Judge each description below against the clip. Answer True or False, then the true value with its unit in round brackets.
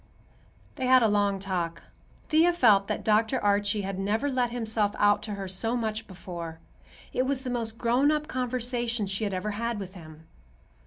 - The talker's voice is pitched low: False (215 Hz)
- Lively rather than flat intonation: False (3.8 semitones)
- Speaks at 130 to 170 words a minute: False (180 wpm)